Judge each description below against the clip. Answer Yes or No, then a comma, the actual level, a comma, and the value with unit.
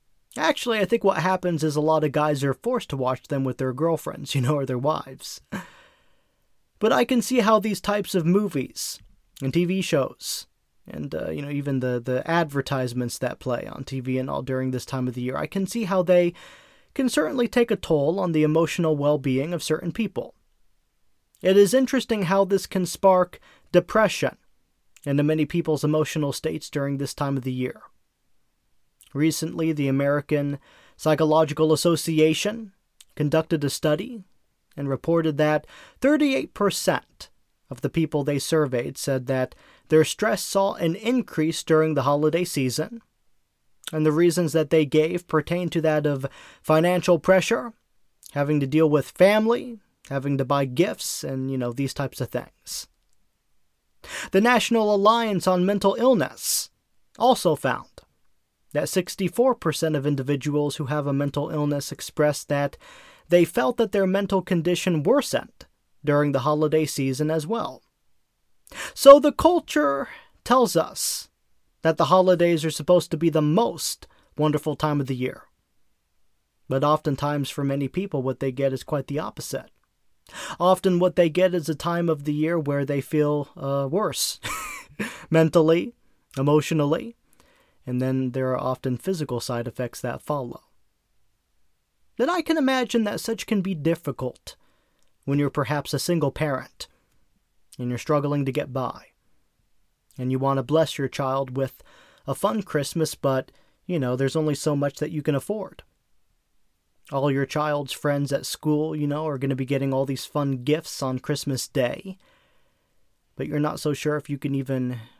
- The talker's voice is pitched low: No, medium, 155 Hz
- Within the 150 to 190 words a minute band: Yes, average, 160 wpm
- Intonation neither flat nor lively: Yes, average, 4.8 semitones